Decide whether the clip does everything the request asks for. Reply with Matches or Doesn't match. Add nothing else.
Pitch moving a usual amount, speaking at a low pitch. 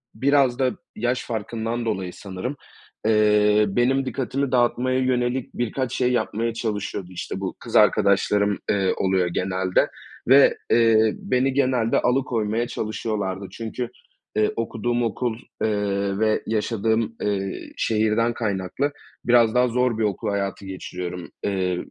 Matches